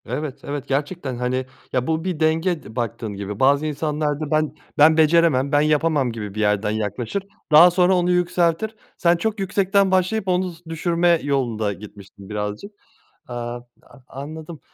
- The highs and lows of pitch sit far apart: Yes, wide, 5.9 semitones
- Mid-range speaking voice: Yes, medium, 150 Hz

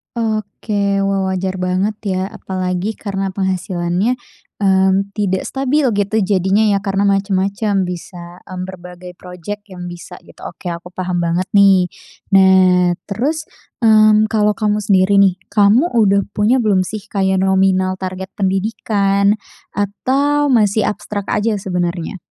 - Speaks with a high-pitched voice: Yes, high, 195 Hz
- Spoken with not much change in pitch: Yes, narrow, 2.1 semitones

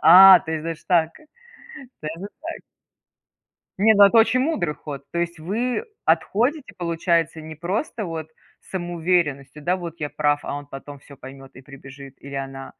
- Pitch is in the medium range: Yes, medium, 165 Hz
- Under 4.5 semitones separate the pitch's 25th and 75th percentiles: No, average, 4.8 semitones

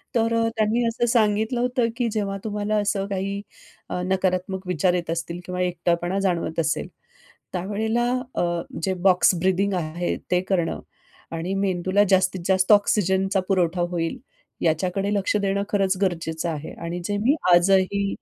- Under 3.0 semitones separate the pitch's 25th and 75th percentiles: Yes, narrow, 2.4 semitones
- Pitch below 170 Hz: No, high, 190 Hz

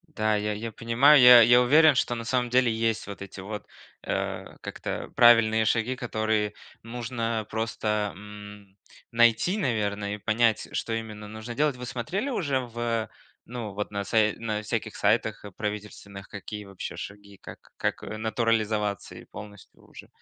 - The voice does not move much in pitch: Yes, narrow, 2.2 semitones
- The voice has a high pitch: No, low, 110 Hz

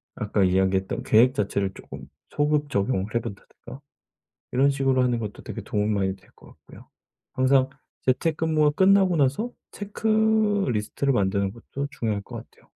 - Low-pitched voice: Yes, low, 130 Hz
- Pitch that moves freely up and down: Yes, wide, 6.7 semitones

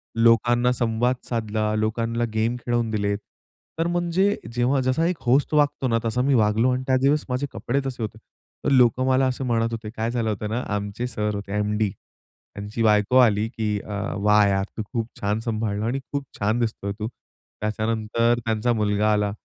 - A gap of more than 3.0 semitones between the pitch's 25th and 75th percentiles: No, average, 2.7 semitones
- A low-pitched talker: Yes, low, 115 Hz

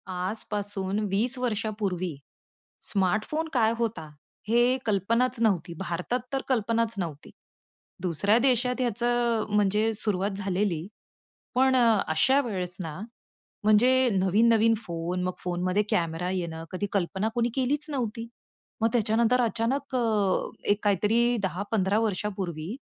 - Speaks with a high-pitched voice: Yes, high, 210 Hz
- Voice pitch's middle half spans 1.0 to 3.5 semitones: No, average, 4.1 semitones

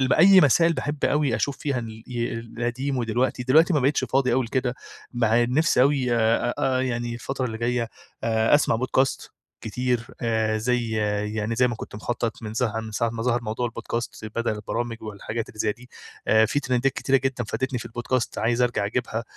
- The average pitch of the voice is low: Yes, low, 120 Hz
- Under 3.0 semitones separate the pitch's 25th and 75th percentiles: Yes, narrow, 2.4 semitones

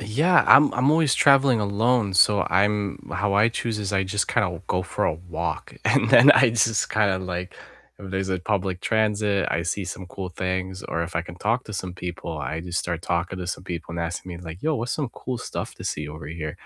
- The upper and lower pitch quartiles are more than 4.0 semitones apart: No, average, 3.7 semitones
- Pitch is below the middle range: Yes, very low, 95 Hz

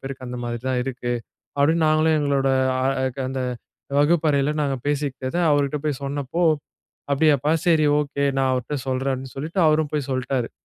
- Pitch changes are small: Yes, narrow, 2.3 semitones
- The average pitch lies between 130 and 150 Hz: Yes, medium, 140 Hz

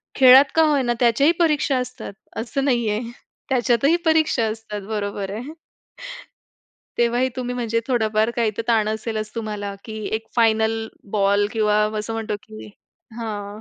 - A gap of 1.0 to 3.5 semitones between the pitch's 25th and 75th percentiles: Yes, average, 2.8 semitones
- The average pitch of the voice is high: Yes, high, 225 Hz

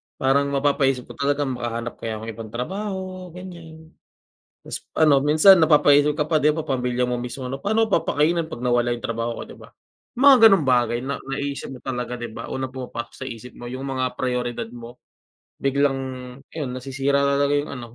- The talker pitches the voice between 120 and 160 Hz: Yes, low, 135 Hz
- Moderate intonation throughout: Yes, average, 3.4 semitones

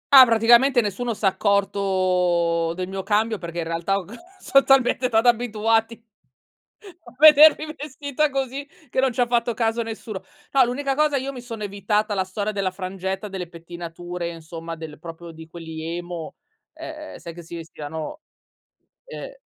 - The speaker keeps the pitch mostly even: No, wide, 6.1 semitones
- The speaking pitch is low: No, high, 205 Hz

